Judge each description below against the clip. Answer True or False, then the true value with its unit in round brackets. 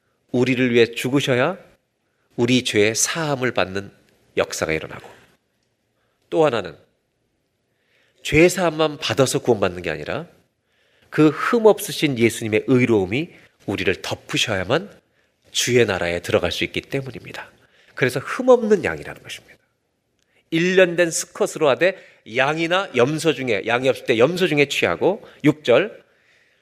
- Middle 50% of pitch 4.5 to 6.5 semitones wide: True (5.5 semitones)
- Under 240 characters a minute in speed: False (280 characters per minute)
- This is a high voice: False (135 Hz)